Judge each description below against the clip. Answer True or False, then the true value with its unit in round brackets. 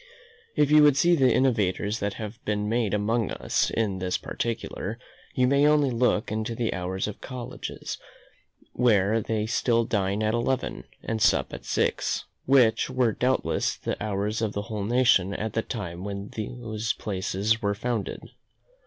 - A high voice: False (110 Hz)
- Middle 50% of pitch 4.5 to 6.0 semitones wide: False (3.2 semitones)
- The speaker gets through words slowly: False (160 wpm)